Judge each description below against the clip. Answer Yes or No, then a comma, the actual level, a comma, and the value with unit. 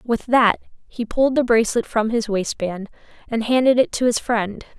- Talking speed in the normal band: Yes, average, 190 wpm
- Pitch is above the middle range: Yes, high, 230 Hz